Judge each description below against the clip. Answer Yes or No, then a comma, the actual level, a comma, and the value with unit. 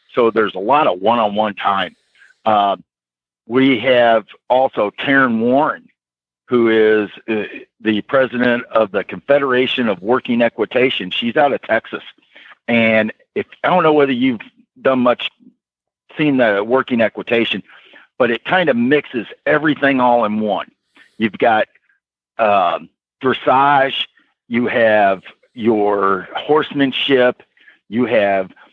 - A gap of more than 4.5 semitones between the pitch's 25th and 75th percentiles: No, average, 3.8 semitones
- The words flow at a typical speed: No, slow, 125 wpm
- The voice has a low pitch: Yes, low, 120 Hz